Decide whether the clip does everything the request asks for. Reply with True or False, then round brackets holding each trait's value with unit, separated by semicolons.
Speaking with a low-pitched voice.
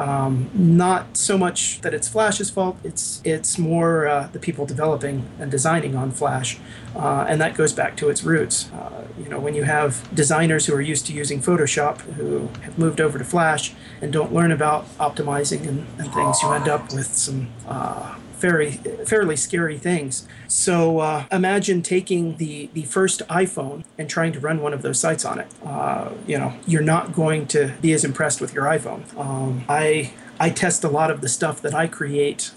False (155 Hz)